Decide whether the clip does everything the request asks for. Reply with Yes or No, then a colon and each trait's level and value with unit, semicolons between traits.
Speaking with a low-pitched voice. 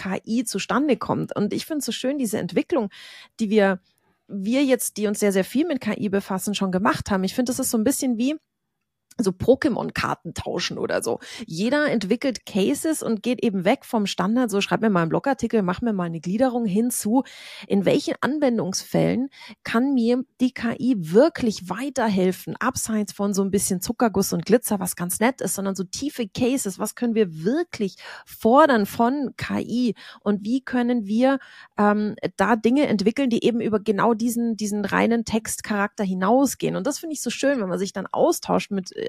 No: high, 230 Hz